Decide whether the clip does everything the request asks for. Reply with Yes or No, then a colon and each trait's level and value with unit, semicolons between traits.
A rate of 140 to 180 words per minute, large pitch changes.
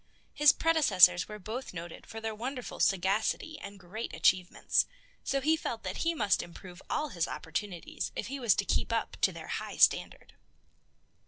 Yes: average, 170 wpm; wide, 6.5 semitones